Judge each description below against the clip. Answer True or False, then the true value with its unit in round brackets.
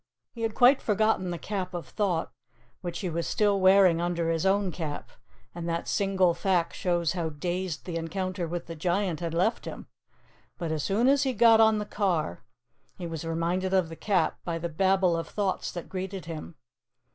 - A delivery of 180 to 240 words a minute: True (190 wpm)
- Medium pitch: True (180 Hz)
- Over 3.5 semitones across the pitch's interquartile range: False (2.8 semitones)